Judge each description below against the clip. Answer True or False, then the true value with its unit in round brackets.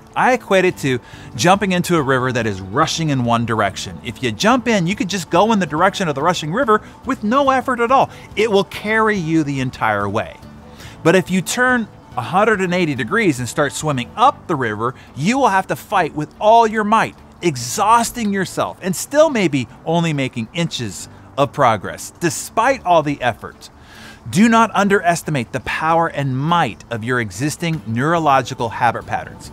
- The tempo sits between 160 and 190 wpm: True (180 wpm)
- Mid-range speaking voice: True (155 Hz)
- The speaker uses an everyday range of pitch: False (8.1 semitones)